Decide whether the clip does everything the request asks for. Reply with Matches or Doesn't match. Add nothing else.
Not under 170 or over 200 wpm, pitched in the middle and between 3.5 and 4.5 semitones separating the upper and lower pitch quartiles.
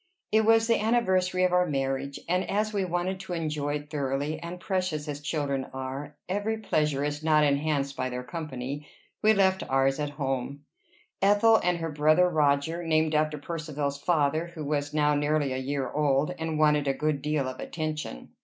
Matches